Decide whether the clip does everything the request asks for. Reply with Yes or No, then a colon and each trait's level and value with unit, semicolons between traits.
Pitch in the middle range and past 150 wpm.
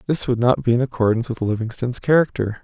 No: low, 120 Hz; fast, 205 wpm